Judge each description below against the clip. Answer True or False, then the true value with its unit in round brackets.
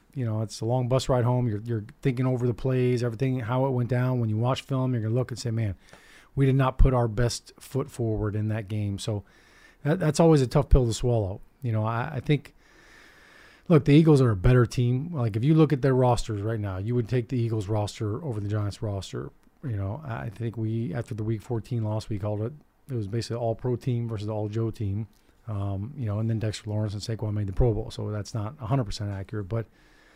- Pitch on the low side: True (115 Hz)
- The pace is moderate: False (245 wpm)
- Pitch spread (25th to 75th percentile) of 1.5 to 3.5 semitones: True (2.9 semitones)